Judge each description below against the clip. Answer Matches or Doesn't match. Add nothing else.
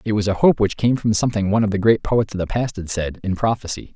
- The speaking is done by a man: Matches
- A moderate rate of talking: Doesn't match